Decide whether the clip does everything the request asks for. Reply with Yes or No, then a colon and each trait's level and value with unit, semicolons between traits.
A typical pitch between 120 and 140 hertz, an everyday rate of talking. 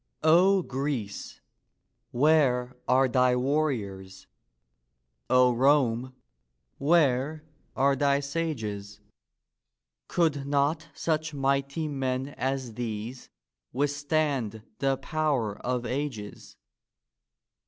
No: low, 135 Hz; slow, 80 wpm